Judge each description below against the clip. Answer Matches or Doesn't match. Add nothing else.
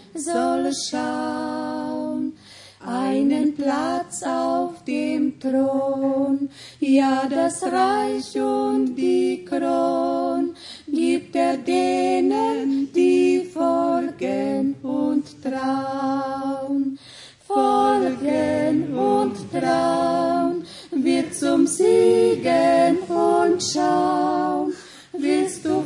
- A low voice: Doesn't match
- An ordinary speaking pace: Doesn't match